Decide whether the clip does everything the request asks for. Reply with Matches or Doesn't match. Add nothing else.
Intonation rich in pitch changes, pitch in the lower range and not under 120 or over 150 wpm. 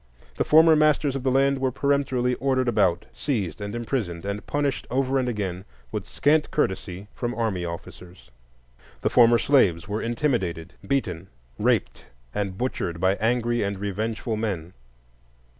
Matches